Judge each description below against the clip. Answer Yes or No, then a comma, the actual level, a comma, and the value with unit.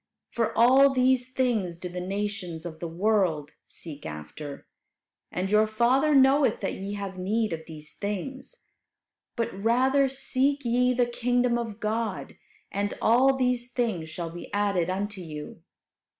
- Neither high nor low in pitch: No, high, 215 Hz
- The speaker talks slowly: No, average, 150 wpm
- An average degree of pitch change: No, wide, 5.7 semitones